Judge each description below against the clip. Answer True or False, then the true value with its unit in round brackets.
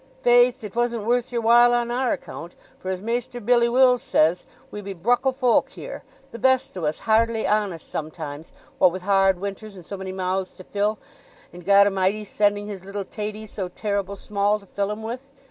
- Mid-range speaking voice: False (210 Hz)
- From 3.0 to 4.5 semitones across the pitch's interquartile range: True (3.9 semitones)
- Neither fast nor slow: True (190 wpm)